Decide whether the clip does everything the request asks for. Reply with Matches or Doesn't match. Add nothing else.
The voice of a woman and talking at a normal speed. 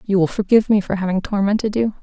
Doesn't match